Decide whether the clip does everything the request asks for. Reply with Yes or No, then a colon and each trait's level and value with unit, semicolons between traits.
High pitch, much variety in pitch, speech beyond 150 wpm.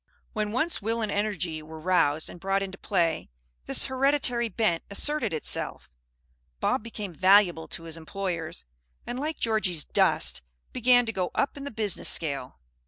Yes: high, 200 Hz; wide, 5.7 semitones; average, 160 wpm